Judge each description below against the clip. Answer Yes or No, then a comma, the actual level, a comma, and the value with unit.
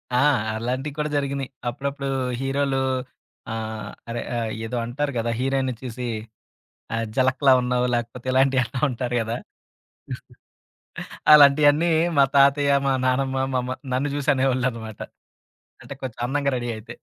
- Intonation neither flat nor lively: No, narrow, 2.2 semitones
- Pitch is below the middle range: Yes, low, 130 Hz